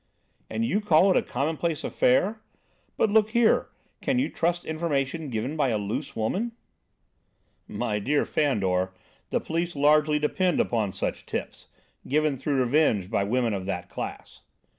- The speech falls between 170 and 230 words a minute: No, average, 150 wpm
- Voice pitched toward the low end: No, medium, 150 Hz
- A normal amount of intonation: No, wide, 6.8 semitones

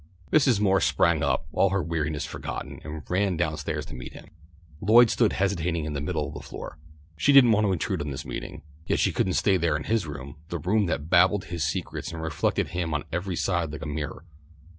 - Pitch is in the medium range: No, very low, 85 Hz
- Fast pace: Yes, fast, 225 wpm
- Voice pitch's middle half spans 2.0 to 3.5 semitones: No, average, 4.2 semitones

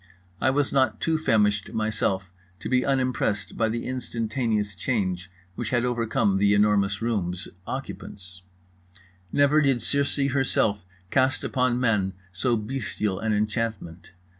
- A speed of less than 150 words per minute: Yes, slow, 135 wpm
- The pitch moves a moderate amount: Yes, average, 4.2 semitones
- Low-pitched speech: Yes, low, 110 Hz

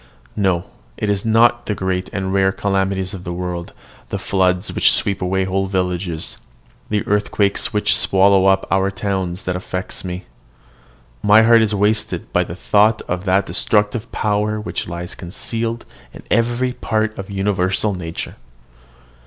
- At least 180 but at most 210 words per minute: No, average, 155 wpm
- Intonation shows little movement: Yes, narrow, 2.2 semitones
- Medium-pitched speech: No, very low, 95 Hz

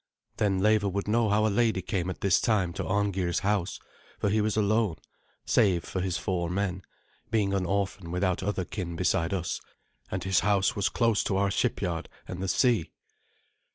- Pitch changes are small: Yes, narrow, 2.2 semitones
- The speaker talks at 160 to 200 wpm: Yes, average, 185 wpm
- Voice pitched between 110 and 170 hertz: No, very low, 95 Hz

